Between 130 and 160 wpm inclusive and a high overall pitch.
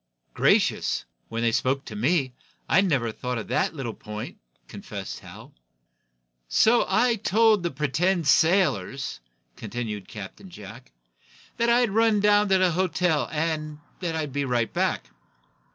No: average, 140 wpm; medium, 155 Hz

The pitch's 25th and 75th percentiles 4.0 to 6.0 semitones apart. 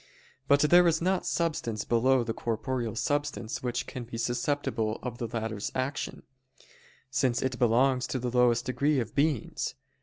No: average, 3.3 semitones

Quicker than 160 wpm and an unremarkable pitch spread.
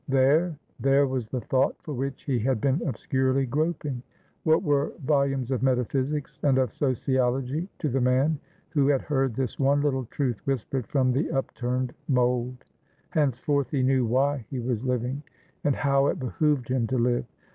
No: average, 170 wpm; narrow, 2.0 semitones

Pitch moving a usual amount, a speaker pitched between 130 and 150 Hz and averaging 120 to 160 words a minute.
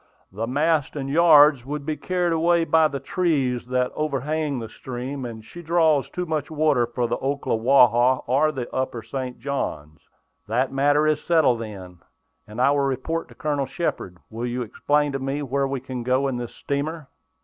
No: average, 3.7 semitones; low, 135 Hz; average, 180 wpm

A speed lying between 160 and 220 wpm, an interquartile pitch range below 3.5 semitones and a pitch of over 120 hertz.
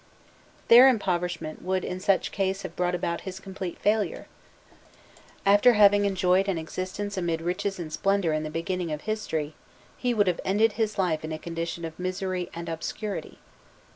Yes: average, 170 wpm; average, 3.0 semitones; medium, 185 Hz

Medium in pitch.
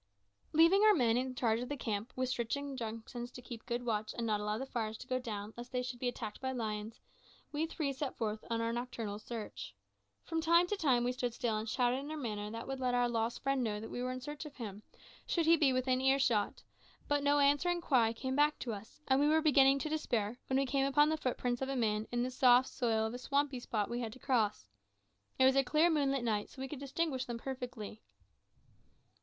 No: very high, 250 Hz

